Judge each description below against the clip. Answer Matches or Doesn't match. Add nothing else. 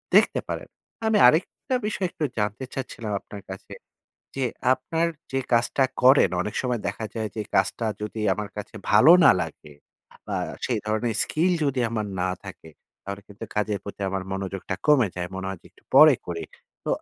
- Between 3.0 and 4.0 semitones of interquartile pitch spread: Doesn't match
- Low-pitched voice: Matches